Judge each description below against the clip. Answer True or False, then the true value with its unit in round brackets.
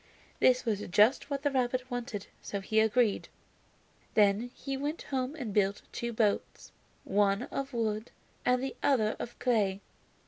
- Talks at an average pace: True (150 wpm)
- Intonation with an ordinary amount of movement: True (3.6 semitones)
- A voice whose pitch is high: True (235 Hz)